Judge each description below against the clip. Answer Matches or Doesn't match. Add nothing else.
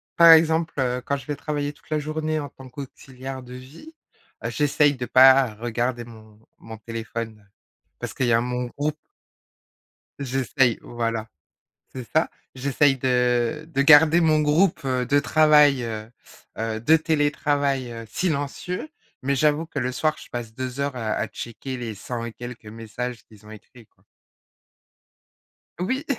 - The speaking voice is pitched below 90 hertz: Doesn't match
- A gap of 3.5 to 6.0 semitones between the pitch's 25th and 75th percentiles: Matches